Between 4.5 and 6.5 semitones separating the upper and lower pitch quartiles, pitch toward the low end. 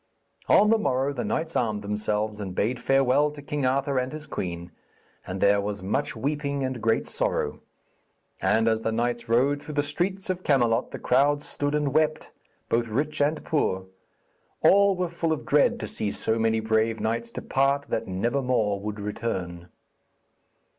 Yes: average, 5.1 semitones; low, 125 Hz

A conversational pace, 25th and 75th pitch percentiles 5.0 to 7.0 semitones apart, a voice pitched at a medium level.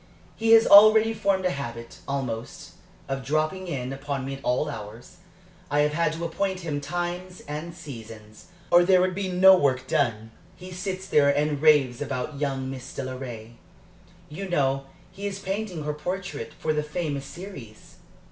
Yes: average, 165 wpm; wide, 5.4 semitones; medium, 150 Hz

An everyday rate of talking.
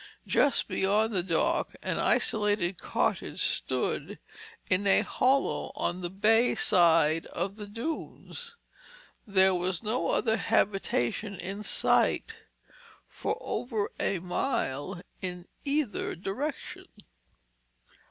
No: slow, 105 wpm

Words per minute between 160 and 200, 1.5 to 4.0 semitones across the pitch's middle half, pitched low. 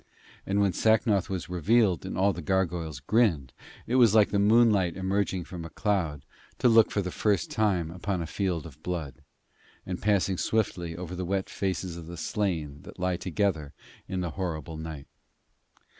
Yes: average, 175 wpm; average, 3.4 semitones; very low, 90 Hz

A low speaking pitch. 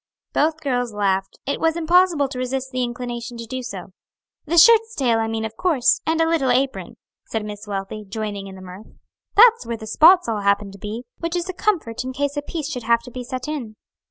No: very high, 250 Hz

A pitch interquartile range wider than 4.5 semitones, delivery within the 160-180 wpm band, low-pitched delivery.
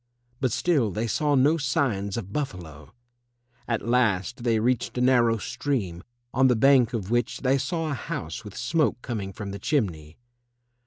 Yes: average, 4.9 semitones; average, 165 wpm; low, 120 Hz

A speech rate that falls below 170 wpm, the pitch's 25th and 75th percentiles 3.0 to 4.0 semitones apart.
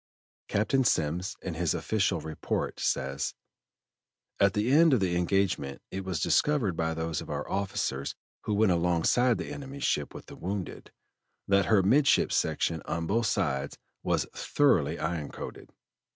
No: average, 150 wpm; average, 5.0 semitones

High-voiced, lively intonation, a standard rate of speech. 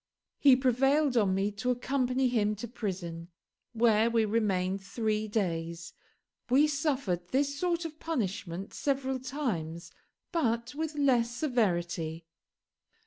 No: high, 230 Hz; wide, 5.8 semitones; slow, 120 wpm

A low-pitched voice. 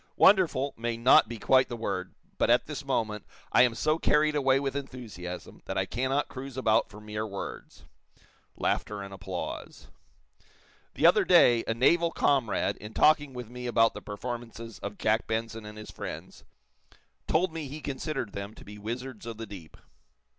Yes: low, 115 Hz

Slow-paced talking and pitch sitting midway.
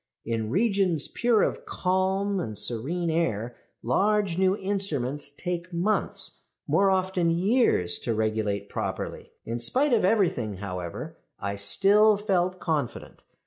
Yes: slow, 125 wpm; medium, 175 Hz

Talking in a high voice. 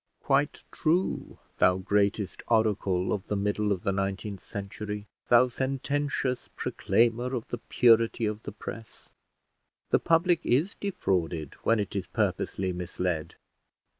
No: low, 105 Hz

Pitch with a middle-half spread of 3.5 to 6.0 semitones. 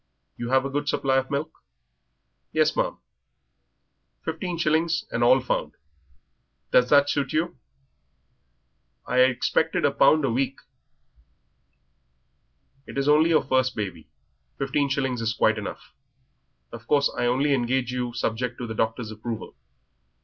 No: average, 3.1 semitones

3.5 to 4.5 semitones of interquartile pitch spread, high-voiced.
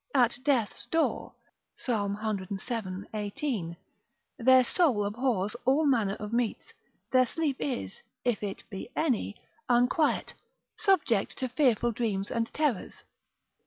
Yes: average, 4.2 semitones; high, 230 Hz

